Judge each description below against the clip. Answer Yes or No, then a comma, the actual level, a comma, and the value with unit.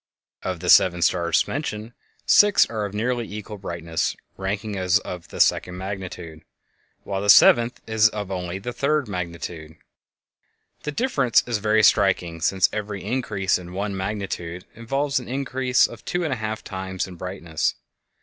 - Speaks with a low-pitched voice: Yes, low, 100 Hz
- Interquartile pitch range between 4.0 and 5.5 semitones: Yes, average, 4.3 semitones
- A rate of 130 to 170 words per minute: Yes, average, 160 wpm